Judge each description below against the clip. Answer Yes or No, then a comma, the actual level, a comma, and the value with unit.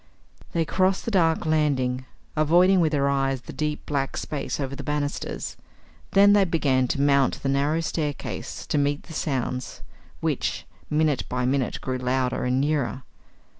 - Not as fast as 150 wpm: No, average, 160 wpm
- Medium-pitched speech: Yes, medium, 145 Hz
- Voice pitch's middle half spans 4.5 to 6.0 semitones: No, average, 3.0 semitones